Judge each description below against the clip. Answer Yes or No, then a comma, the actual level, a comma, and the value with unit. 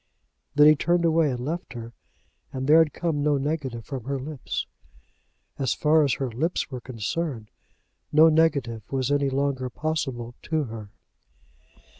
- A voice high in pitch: No, medium, 140 Hz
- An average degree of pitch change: Yes, average, 3.7 semitones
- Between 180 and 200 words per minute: No, average, 155 wpm